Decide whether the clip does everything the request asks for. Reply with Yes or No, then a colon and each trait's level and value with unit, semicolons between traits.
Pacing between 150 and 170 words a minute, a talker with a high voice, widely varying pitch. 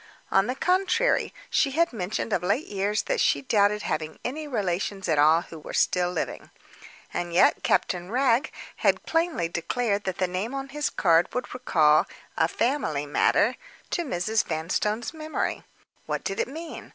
Yes: average, 165 wpm; high, 205 Hz; wide, 7.7 semitones